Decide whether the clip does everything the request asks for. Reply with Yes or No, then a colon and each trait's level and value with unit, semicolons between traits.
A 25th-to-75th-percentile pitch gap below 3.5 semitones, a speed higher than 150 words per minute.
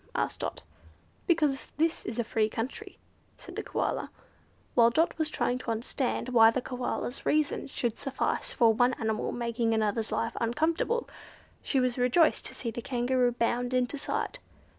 Yes: average, 2.8 semitones; average, 160 wpm